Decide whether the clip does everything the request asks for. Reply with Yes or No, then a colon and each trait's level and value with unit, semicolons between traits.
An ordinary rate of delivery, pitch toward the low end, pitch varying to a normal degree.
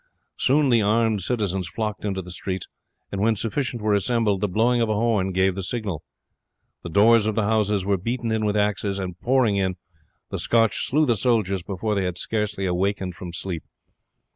Yes: average, 190 wpm; low, 105 Hz; average, 3.1 semitones